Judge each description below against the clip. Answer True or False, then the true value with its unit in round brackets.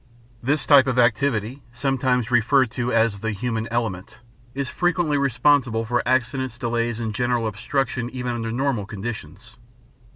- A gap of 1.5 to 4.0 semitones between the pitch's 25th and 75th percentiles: True (2.7 semitones)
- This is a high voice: False (120 Hz)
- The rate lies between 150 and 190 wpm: False (140 wpm)